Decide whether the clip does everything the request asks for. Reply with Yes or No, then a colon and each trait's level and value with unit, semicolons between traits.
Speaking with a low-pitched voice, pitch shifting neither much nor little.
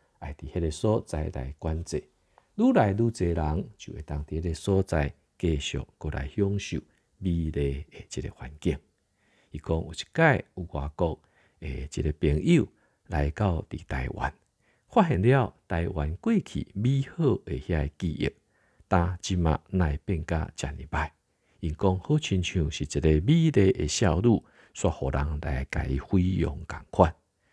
Yes: very low, 80 Hz; average, 4.2 semitones